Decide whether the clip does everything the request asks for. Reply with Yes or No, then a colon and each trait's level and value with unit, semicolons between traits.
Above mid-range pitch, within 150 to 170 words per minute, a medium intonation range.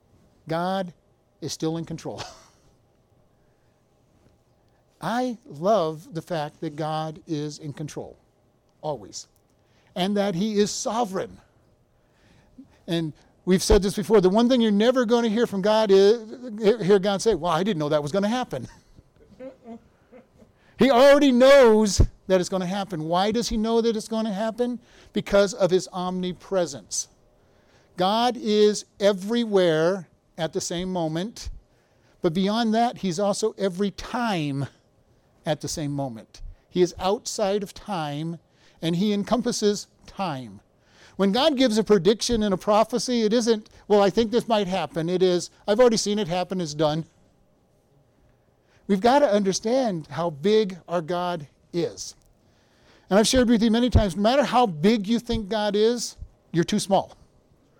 Yes: high, 200 Hz; average, 155 wpm; average, 4.7 semitones